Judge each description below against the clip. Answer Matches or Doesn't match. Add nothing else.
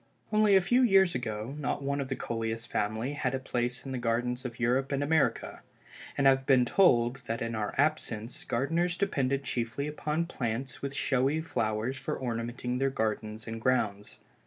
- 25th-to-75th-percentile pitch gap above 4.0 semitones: Doesn't match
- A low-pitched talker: Matches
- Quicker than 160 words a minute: Matches